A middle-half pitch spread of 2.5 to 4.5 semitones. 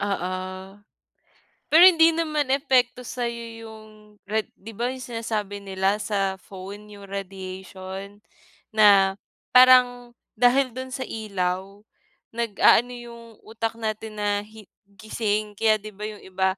Yes: average, 3.3 semitones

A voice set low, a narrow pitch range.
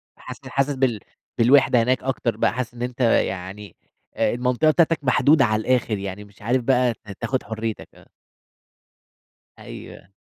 No: low, 120 Hz; average, 3.0 semitones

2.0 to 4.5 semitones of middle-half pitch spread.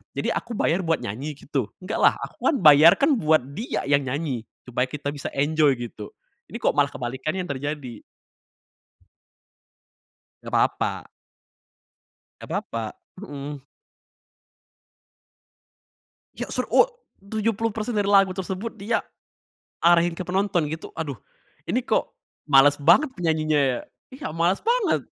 No: wide, 5.6 semitones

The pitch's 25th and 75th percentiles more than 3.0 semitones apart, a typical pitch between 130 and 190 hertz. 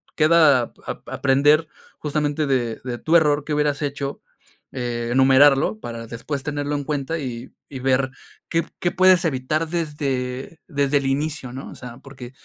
No: average, 2.7 semitones; medium, 140 Hz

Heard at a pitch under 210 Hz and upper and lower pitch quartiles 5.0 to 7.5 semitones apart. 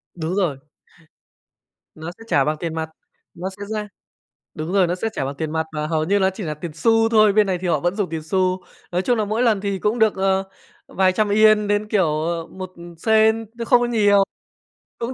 No: high, 190 Hz; average, 4.3 semitones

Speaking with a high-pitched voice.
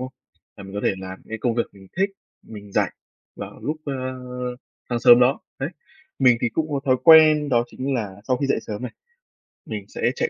No: low, 125 Hz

